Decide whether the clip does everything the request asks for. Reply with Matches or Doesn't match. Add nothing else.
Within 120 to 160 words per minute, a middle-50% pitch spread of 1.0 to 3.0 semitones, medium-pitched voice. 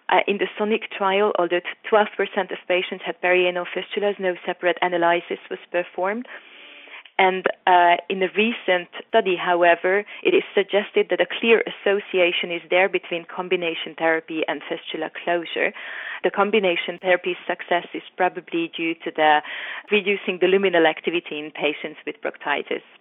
Matches